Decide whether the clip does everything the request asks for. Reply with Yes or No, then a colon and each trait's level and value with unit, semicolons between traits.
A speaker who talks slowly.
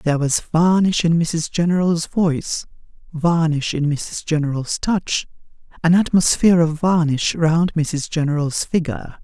Yes: slow, 130 wpm